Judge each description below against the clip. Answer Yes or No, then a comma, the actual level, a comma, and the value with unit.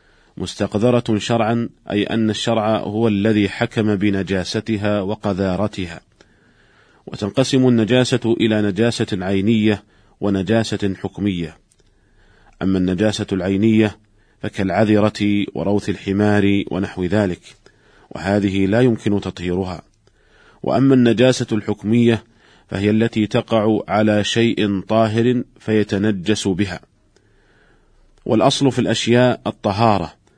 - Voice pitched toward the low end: Yes, low, 105 Hz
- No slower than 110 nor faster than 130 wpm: No, average, 85 wpm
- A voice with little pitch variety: Yes, narrow, 2.2 semitones